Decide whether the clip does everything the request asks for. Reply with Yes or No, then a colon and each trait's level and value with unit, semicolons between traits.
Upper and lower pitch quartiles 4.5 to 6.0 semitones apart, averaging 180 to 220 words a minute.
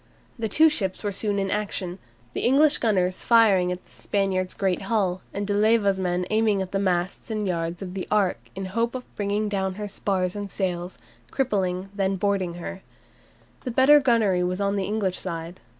No: narrow, 2.4 semitones; average, 200 wpm